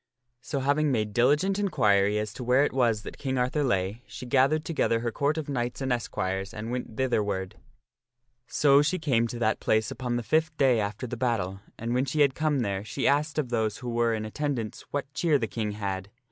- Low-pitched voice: Yes, low, 120 Hz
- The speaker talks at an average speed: No, fast, 215 wpm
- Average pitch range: Yes, average, 4.7 semitones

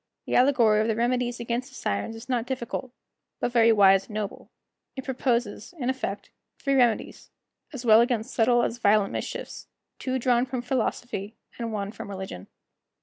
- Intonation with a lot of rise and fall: No, average, 2.7 semitones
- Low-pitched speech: No, high, 235 Hz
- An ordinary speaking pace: Yes, average, 170 wpm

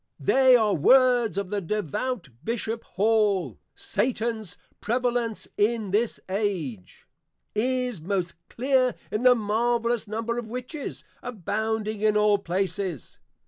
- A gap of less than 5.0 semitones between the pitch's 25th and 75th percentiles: Yes, average, 3.2 semitones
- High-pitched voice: Yes, high, 220 Hz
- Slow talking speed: Yes, slow, 115 wpm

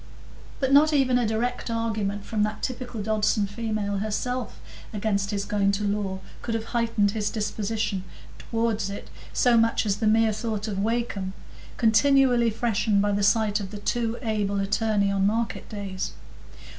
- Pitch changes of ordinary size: No, narrow, 2.2 semitones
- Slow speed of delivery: No, average, 160 wpm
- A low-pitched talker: No, high, 215 Hz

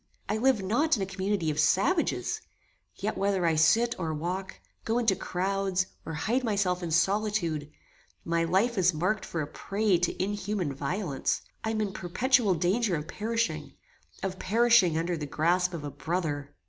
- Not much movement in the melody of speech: No, average, 4.3 semitones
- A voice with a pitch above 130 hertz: Yes, high, 190 Hz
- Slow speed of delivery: No, average, 170 wpm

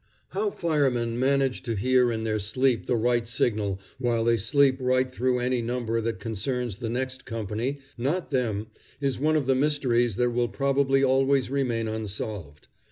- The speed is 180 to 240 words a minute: No, average, 165 wpm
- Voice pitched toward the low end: Yes, low, 125 Hz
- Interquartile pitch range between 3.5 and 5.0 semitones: No, average, 2.8 semitones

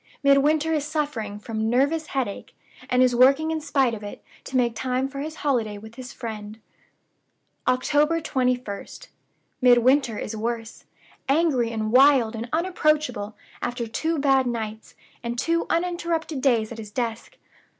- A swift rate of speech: No, average, 145 wpm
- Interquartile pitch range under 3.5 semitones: No, average, 4.7 semitones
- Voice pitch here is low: No, very high, 255 Hz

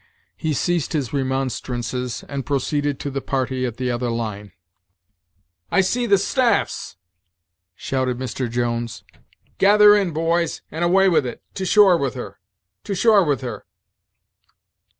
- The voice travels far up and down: Yes, wide, 6.2 semitones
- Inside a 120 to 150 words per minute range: Yes, average, 140 wpm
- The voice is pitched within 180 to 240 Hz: No, medium, 140 Hz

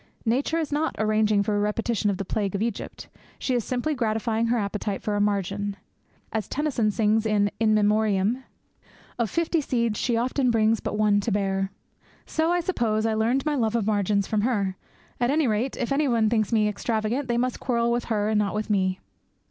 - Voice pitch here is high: Yes, high, 220 Hz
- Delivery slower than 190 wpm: No, average, 200 wpm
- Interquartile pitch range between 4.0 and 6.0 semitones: No, narrow, 2.6 semitones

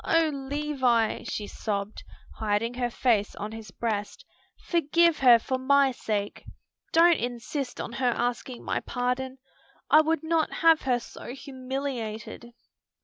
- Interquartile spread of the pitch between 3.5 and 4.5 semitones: Yes, average, 3.9 semitones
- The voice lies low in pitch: No, very high, 255 Hz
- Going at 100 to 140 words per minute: Yes, slow, 135 wpm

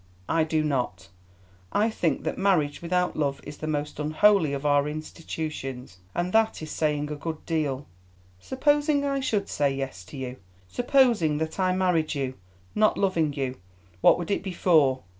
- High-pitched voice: No, medium, 155 Hz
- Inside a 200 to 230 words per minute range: No, average, 170 wpm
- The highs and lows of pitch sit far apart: No, average, 4.7 semitones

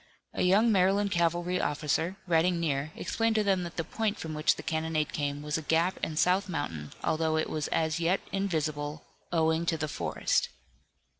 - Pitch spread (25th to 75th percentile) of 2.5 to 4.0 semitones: Yes, average, 3.0 semitones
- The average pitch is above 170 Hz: No, medium, 165 Hz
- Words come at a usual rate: Yes, average, 180 wpm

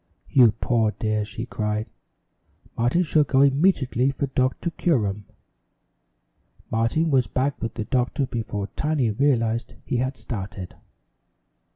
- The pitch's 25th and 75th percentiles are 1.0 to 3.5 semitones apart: No, average, 4.0 semitones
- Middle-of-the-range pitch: No, low, 125 Hz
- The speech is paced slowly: Yes, slow, 120 wpm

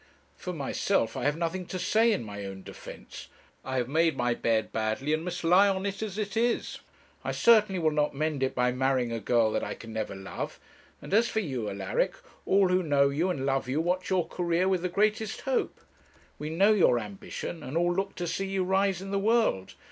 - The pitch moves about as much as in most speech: No, wide, 7.0 semitones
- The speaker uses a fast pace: Yes, fast, 220 wpm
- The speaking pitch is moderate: Yes, medium, 165 Hz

